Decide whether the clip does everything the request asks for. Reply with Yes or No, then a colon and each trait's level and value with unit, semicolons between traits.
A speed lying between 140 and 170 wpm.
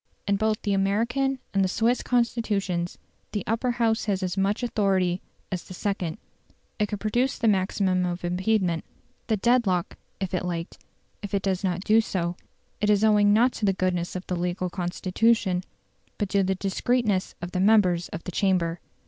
No: average, 180 wpm